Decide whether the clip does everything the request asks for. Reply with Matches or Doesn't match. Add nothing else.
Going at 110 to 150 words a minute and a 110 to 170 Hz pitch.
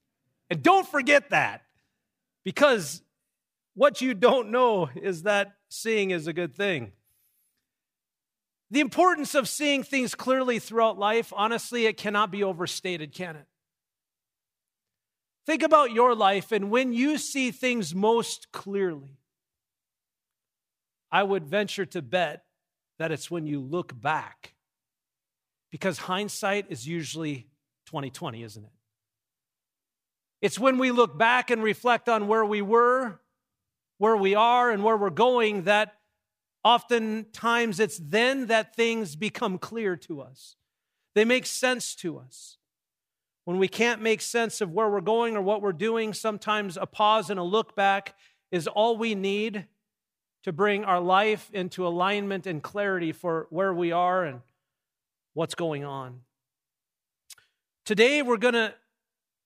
Doesn't match